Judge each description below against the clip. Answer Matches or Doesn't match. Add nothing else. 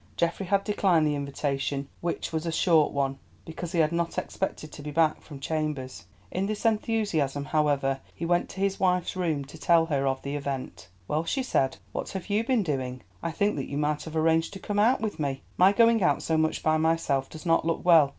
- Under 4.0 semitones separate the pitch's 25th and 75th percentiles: Doesn't match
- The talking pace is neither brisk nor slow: Doesn't match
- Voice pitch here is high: Doesn't match